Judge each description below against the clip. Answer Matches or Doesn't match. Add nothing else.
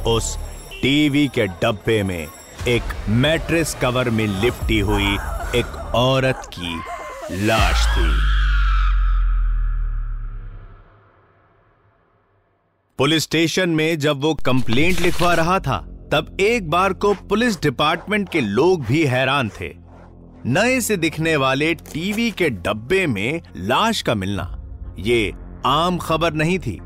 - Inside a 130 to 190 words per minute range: Doesn't match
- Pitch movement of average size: Doesn't match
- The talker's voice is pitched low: Matches